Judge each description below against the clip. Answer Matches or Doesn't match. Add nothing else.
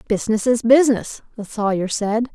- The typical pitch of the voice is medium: Doesn't match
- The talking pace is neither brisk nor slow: Matches